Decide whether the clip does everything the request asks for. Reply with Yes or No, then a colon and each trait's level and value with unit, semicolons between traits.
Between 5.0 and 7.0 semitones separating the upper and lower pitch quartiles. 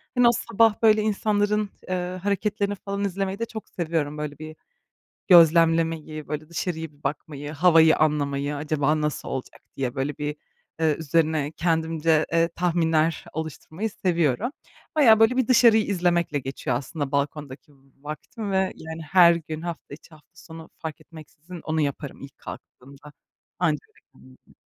No: average, 3.7 semitones